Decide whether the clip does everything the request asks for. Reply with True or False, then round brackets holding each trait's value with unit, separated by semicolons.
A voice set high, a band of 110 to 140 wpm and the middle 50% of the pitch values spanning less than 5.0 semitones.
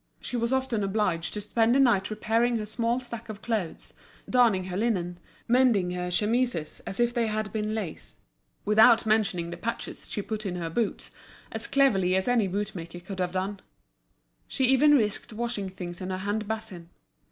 False (215 Hz; 180 wpm; 3.8 semitones)